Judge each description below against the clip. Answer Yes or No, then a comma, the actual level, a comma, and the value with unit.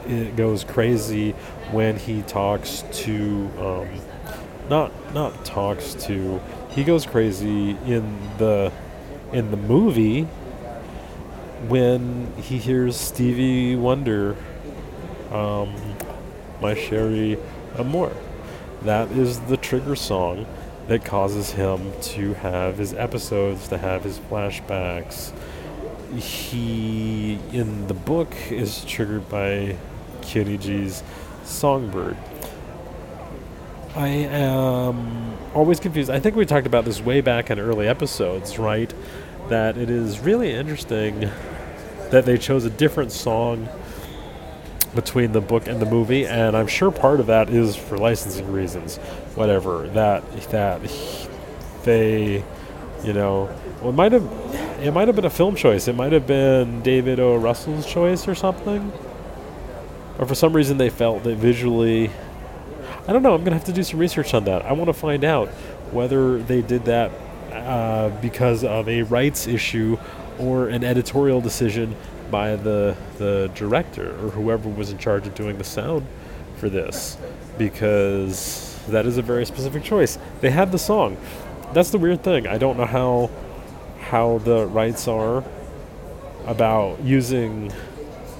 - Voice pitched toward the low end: Yes, low, 115 Hz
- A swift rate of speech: No, average, 140 wpm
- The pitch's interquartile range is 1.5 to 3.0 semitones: No, average, 4.1 semitones